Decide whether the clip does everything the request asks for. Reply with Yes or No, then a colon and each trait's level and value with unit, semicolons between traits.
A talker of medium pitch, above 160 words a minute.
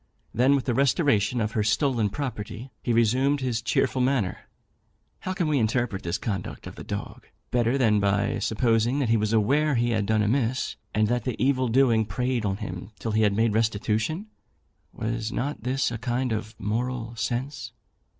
No: low, 115 Hz; average, 180 wpm